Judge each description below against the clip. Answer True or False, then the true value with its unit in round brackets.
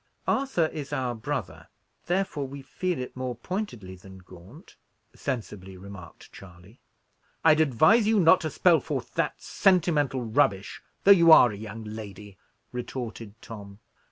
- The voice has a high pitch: False (125 Hz)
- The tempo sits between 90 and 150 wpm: True (140 wpm)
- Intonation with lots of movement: True (8.1 semitones)